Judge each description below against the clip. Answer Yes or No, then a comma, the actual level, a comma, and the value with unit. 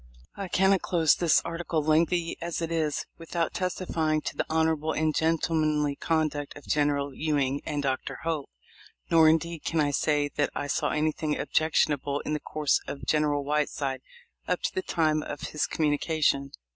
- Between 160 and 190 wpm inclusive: Yes, average, 170 wpm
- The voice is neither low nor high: Yes, medium, 155 Hz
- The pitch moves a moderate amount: No, narrow, 2.0 semitones